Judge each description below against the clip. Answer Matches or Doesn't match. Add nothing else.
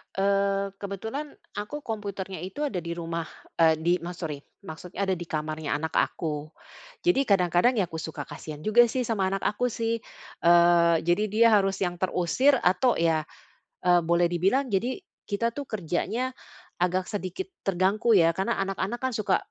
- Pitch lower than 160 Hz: Doesn't match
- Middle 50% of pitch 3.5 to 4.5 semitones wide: Matches